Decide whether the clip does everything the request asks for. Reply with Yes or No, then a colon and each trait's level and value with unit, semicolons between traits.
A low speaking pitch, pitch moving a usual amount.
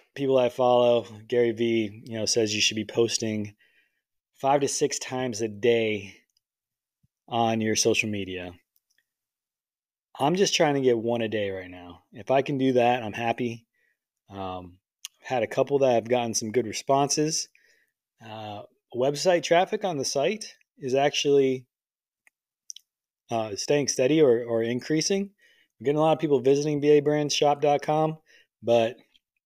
Yes: low, 125 Hz; average, 4.4 semitones